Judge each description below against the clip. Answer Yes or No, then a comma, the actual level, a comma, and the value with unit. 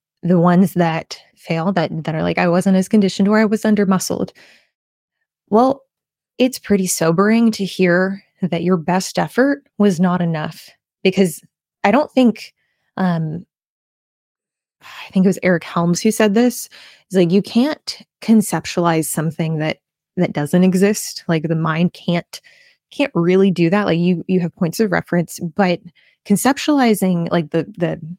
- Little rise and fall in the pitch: No, average, 4.0 semitones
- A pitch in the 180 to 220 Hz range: Yes, medium, 185 Hz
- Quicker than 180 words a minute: No, average, 160 wpm